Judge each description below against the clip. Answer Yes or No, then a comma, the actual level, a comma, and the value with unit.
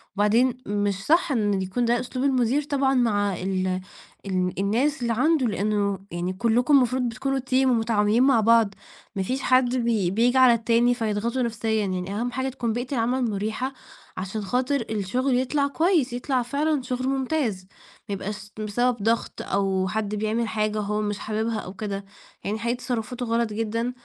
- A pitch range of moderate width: Yes, average, 3.6 semitones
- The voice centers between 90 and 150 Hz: No, high, 230 Hz